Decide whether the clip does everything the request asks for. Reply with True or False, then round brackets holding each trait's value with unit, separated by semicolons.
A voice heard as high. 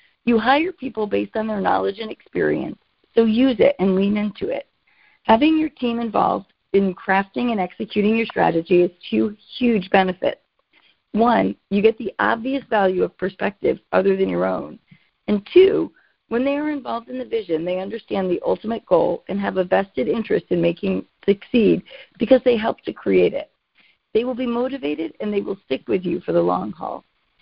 True (215 Hz)